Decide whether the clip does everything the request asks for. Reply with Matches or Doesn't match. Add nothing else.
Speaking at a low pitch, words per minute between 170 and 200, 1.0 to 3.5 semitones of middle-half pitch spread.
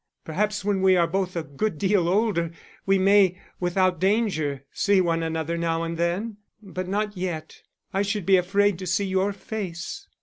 Doesn't match